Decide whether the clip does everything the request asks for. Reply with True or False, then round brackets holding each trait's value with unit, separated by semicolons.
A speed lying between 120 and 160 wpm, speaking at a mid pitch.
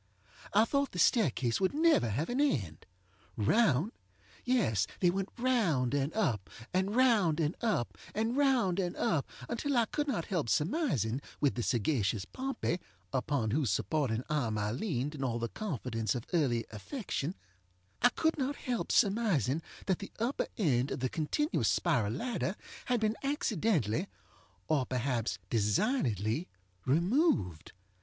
True (145 wpm; 160 Hz)